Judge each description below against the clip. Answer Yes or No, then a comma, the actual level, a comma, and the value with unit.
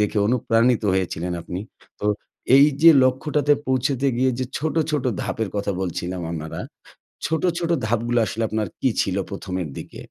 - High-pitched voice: No, low, 115 Hz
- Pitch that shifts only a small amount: No, wide, 5.5 semitones